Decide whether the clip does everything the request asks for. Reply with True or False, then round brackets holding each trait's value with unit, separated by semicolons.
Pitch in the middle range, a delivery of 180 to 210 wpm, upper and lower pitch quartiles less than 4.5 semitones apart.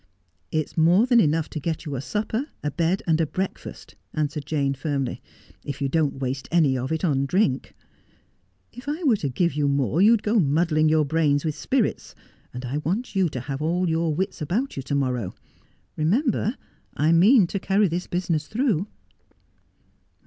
False (160 Hz; 185 wpm; 5.1 semitones)